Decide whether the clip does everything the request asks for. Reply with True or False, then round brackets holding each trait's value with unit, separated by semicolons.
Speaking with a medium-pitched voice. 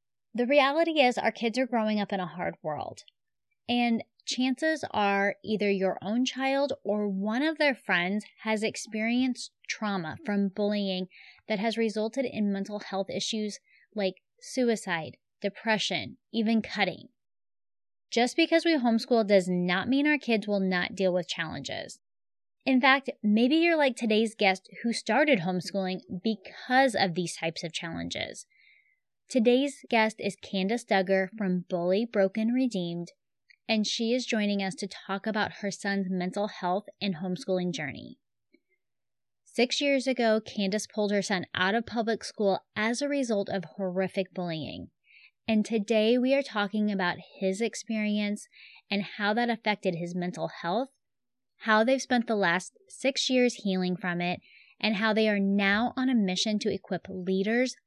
False (210 Hz)